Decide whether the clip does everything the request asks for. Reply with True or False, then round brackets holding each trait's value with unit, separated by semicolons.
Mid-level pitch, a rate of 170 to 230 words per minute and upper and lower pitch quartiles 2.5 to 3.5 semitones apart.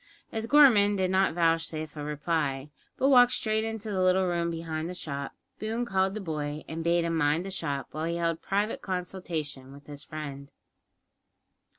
False (170 Hz; 180 wpm; 4.2 semitones)